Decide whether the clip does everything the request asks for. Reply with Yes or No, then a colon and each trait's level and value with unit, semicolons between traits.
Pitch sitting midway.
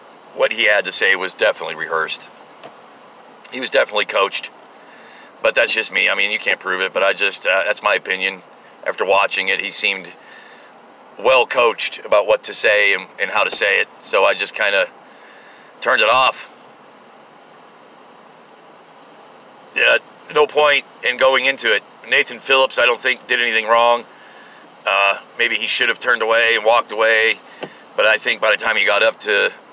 Yes: medium, 150 Hz